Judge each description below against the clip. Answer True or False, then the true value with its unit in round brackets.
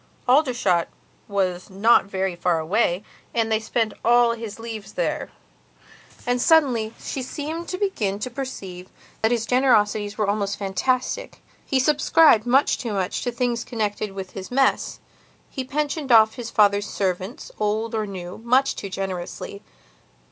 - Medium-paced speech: True (150 wpm)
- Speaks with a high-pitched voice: True (220 Hz)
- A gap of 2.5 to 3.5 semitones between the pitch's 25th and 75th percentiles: False (4.1 semitones)